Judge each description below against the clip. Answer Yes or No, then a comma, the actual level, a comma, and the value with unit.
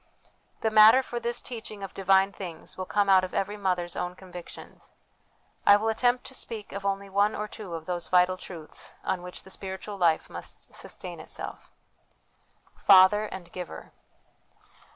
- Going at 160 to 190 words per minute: Yes, average, 165 wpm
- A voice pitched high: Yes, high, 195 Hz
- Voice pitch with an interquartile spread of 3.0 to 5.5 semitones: No, narrow, 2.6 semitones